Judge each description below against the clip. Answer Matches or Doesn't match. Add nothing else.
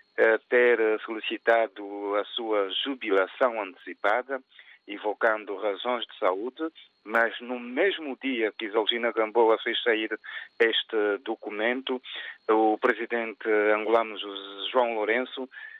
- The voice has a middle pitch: Doesn't match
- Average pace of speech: Doesn't match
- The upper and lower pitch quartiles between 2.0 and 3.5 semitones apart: Matches